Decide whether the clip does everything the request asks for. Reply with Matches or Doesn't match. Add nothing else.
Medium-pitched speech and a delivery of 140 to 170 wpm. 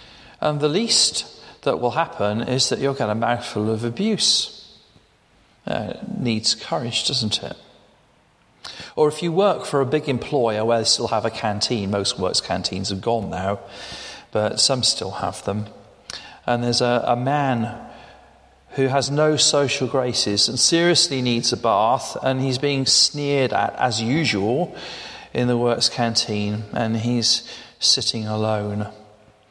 Doesn't match